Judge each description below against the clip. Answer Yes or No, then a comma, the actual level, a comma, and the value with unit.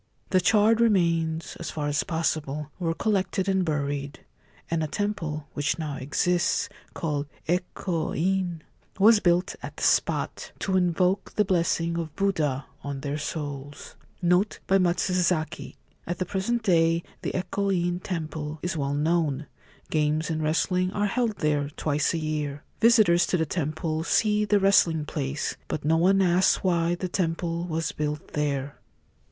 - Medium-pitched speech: Yes, medium, 165 Hz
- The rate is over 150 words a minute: Yes, average, 160 wpm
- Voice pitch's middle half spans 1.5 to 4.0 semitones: Yes, average, 3.5 semitones